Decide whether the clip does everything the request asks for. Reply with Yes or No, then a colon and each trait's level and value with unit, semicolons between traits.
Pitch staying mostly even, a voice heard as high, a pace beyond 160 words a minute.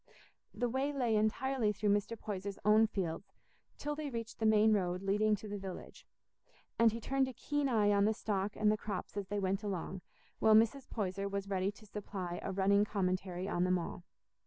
Yes: narrow, 2.3 semitones; high, 205 Hz; average, 200 wpm